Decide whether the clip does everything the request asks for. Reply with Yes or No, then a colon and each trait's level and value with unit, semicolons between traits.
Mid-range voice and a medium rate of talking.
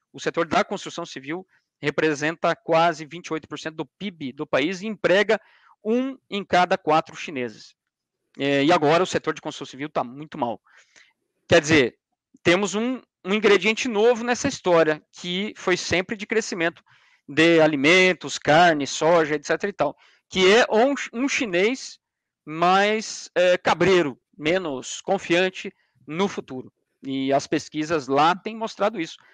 Yes: medium, 170 Hz; average, 140 wpm